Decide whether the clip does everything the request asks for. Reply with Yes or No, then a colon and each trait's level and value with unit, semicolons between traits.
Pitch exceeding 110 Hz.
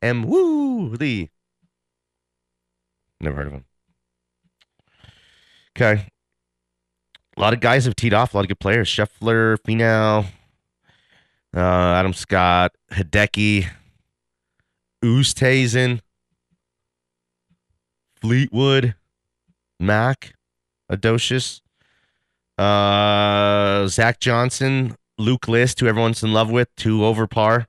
No: low, 105 Hz